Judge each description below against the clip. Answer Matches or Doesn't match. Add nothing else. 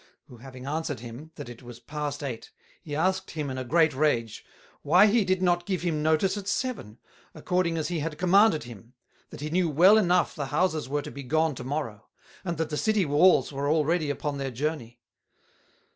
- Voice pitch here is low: Doesn't match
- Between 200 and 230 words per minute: Matches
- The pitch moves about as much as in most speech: Matches